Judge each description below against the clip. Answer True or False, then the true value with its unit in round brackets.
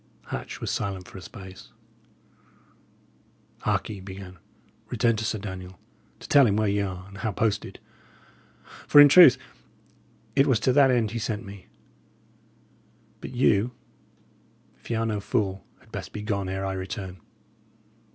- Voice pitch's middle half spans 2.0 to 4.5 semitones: True (3.3 semitones)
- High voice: False (100 Hz)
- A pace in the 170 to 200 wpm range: False (160 wpm)